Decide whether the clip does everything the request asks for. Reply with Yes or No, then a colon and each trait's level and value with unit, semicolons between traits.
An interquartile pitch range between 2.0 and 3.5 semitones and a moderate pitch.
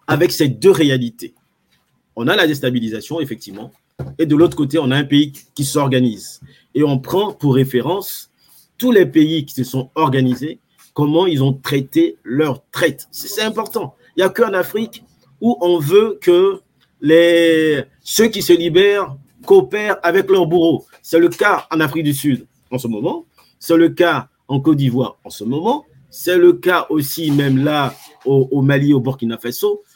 No: average, 4.8 semitones; medium, 155 Hz